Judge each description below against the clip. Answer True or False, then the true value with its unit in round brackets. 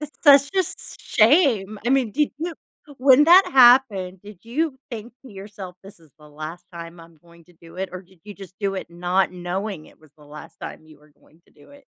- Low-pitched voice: False (195 Hz)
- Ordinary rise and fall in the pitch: False (7.2 semitones)